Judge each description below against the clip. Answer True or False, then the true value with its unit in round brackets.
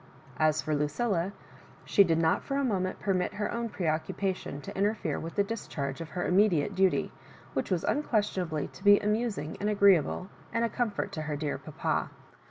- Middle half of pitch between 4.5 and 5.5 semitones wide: True (4.8 semitones)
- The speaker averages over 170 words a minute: True (185 wpm)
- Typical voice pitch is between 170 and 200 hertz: True (190 Hz)